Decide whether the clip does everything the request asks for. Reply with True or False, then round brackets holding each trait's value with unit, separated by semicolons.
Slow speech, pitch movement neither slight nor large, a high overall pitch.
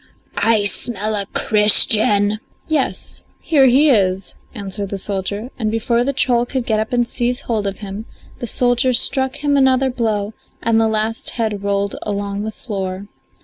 False (165 wpm; 3.3 semitones; 220 Hz)